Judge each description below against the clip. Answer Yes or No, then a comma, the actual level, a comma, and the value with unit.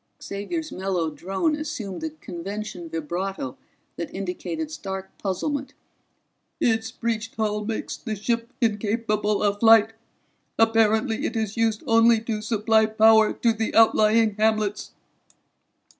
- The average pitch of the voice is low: No, high, 220 Hz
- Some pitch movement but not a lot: No, narrow, 2.2 semitones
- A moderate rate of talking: No, slow, 120 wpm